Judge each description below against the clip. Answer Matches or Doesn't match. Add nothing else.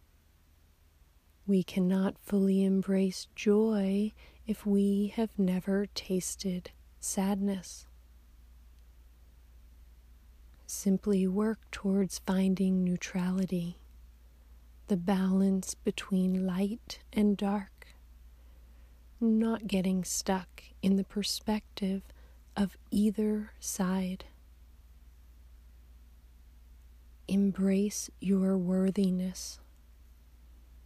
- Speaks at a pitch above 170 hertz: Matches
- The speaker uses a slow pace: Matches